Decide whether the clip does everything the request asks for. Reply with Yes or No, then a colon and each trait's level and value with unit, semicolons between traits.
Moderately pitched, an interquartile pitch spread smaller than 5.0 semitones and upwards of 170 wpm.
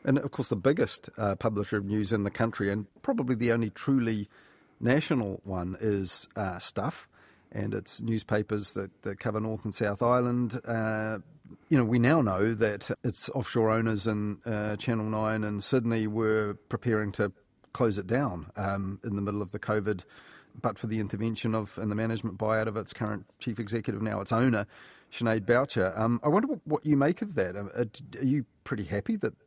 No: low, 110 Hz; average, 2.8 semitones; average, 190 wpm